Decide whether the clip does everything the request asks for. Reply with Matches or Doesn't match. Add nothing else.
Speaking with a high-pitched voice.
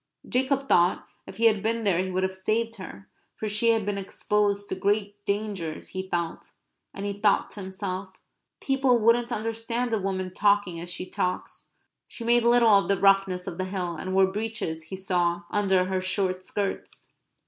Matches